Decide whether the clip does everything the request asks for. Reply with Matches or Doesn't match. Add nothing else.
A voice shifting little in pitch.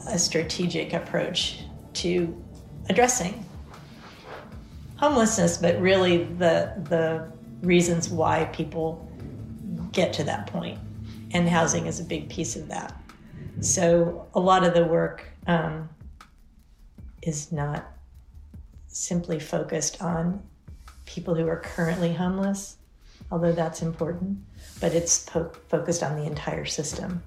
Matches